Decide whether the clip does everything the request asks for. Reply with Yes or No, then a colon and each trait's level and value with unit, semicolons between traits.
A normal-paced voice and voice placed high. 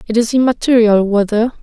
Yes: average, 150 wpm; high, 225 Hz